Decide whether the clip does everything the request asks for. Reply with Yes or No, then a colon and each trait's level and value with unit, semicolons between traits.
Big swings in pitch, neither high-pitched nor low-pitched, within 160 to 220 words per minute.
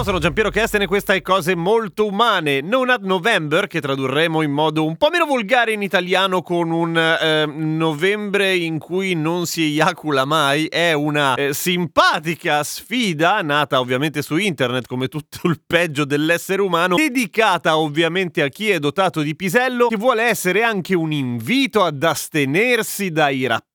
No: average, 4.6 semitones; medium, 170 Hz; average, 165 wpm